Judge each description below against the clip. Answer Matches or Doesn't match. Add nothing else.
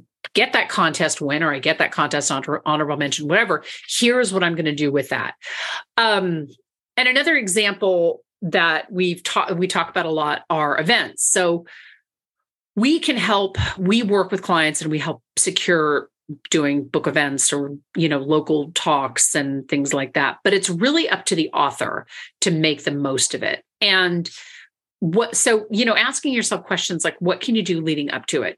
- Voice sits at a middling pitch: Matches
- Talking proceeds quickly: Doesn't match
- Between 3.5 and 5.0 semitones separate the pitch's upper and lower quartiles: Doesn't match